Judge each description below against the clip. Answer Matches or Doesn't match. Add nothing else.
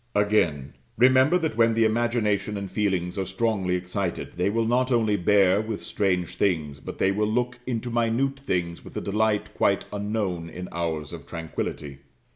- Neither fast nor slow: Matches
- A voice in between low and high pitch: Doesn't match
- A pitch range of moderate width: Matches